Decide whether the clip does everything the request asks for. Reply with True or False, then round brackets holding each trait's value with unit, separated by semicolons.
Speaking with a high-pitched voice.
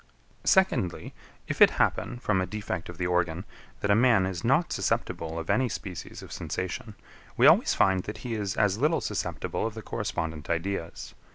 False (95 Hz)